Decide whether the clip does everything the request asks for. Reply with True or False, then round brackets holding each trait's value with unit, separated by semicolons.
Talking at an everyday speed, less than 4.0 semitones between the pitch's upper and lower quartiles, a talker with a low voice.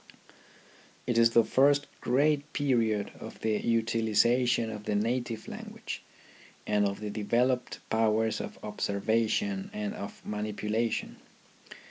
False (115 wpm; 2.9 semitones; 115 Hz)